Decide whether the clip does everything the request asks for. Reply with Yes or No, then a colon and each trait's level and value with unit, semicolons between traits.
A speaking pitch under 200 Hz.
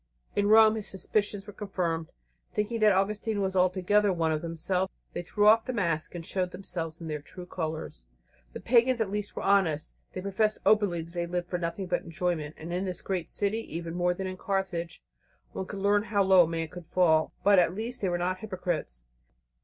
Yes: medium, 185 Hz